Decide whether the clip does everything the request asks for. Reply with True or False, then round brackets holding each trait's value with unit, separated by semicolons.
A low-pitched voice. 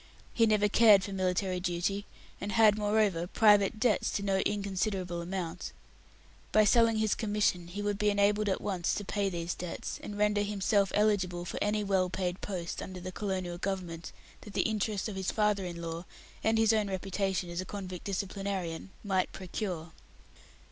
False (195 Hz)